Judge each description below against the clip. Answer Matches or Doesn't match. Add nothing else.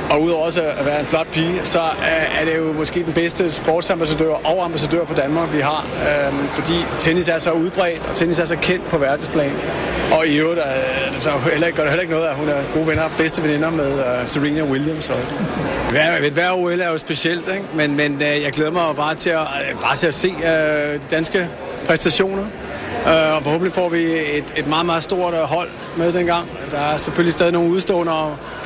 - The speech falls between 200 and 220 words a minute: Matches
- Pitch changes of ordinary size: Doesn't match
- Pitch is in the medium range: Matches